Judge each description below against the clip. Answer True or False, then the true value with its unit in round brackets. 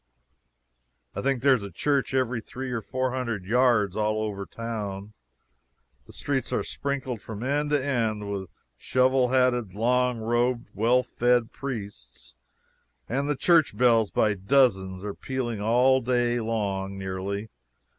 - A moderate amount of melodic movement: True (3.9 semitones)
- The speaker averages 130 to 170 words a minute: True (145 wpm)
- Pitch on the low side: True (120 Hz)